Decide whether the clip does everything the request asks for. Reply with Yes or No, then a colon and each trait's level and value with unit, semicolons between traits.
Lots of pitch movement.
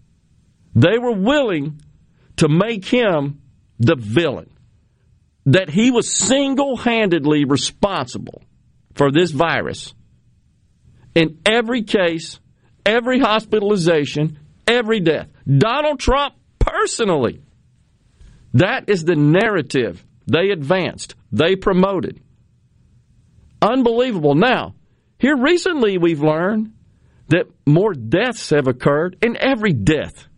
Yes: wide, 8.5 semitones